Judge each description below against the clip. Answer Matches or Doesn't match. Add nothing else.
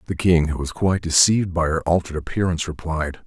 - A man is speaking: Matches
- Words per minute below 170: Doesn't match